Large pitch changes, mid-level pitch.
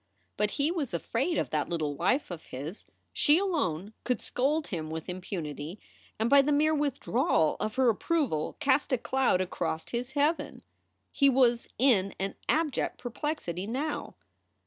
No: wide, 8.2 semitones; high, 245 Hz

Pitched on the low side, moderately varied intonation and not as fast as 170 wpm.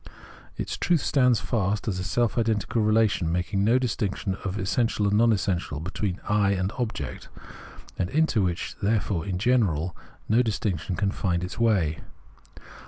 Yes: low, 100 Hz; average, 3.7 semitones; average, 155 wpm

